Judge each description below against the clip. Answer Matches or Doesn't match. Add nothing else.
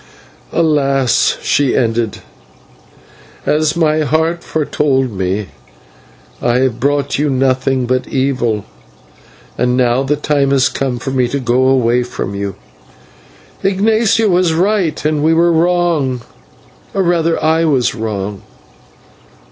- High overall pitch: Doesn't match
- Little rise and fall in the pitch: Doesn't match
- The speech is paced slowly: Matches